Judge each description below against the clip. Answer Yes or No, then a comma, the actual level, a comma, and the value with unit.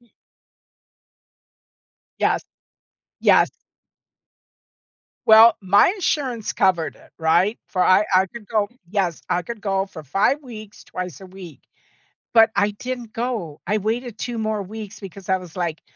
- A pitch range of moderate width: Yes, average, 3.5 semitones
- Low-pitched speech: No, high, 205 Hz